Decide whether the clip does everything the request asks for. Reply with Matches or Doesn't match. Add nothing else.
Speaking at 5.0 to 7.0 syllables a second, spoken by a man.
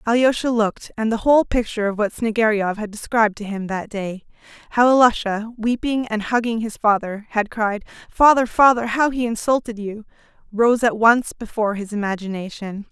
Doesn't match